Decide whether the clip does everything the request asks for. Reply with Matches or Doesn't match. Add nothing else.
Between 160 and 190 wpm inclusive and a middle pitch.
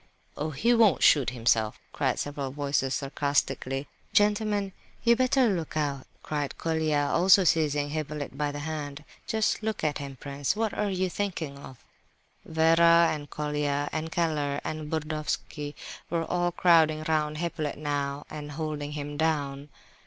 Doesn't match